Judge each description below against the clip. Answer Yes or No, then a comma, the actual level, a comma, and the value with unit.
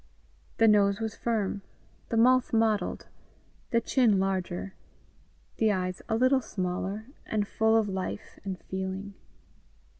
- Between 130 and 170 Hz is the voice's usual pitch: No, high, 205 Hz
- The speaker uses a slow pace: Yes, slow, 125 wpm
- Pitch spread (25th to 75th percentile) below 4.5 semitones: Yes, average, 2.9 semitones